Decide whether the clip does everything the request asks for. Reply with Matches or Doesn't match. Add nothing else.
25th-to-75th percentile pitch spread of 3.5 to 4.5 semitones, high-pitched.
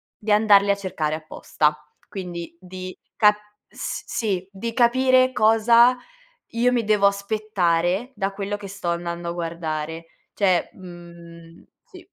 Matches